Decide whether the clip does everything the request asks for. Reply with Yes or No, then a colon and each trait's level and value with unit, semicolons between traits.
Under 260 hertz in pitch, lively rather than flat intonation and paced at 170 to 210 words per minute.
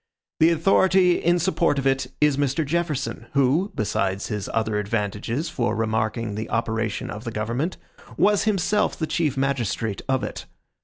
No: low, 135 Hz; wide, 7.0 semitones; average, 155 wpm